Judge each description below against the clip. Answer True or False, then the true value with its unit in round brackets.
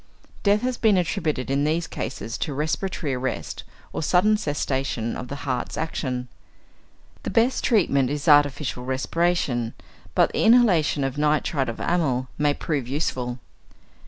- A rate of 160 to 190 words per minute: False (140 wpm)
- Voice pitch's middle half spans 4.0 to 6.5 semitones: True (4.7 semitones)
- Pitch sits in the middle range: True (145 Hz)